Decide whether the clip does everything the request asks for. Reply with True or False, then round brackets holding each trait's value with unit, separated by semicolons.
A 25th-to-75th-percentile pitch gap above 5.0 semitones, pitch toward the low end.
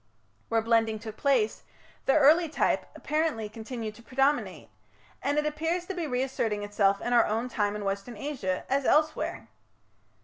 False (5.5 semitones; 240 Hz)